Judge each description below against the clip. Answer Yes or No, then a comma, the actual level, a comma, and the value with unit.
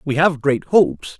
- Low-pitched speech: No, medium, 155 Hz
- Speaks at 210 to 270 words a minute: No, average, 200 wpm